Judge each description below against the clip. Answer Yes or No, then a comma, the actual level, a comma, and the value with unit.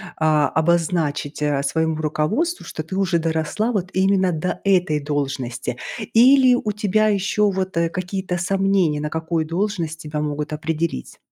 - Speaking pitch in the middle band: Yes, medium, 170 Hz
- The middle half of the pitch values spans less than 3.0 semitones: No, average, 4.1 semitones